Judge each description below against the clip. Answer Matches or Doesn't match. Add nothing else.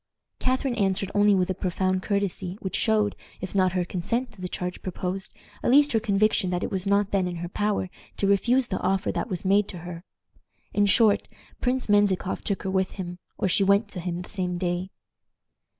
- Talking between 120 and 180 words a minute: Doesn't match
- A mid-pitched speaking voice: Doesn't match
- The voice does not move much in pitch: Matches